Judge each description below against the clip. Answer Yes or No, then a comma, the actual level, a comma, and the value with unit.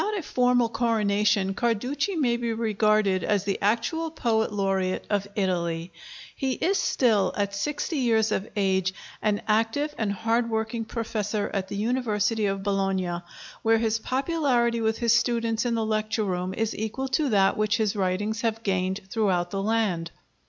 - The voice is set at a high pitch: Yes, high, 220 Hz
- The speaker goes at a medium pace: Yes, average, 165 wpm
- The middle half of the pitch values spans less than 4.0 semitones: Yes, average, 3.0 semitones